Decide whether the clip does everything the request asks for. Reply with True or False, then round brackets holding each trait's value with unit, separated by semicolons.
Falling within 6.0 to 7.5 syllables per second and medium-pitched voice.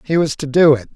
True (6.2 syllables/s; 145 Hz)